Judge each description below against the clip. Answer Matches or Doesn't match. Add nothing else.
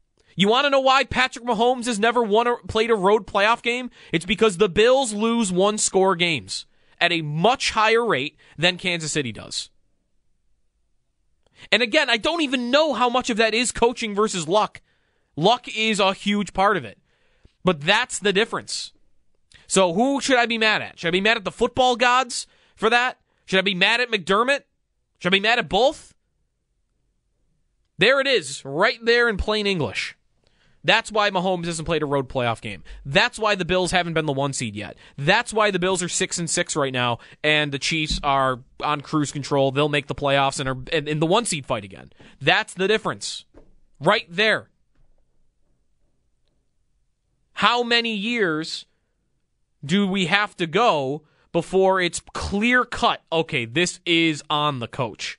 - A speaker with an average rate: Matches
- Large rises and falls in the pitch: Matches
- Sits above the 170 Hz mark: Matches